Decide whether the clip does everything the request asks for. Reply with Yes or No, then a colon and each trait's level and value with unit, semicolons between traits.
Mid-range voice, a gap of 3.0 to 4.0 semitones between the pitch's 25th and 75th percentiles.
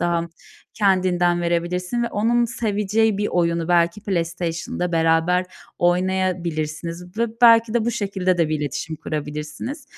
Yes: medium, 180 Hz; average, 3.6 semitones